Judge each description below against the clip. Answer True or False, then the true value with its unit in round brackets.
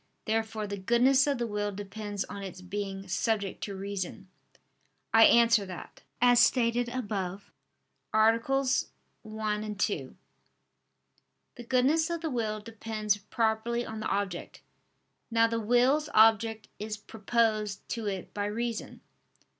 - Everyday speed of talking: False (130 wpm)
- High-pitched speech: True (220 Hz)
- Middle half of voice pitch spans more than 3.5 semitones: False (2.5 semitones)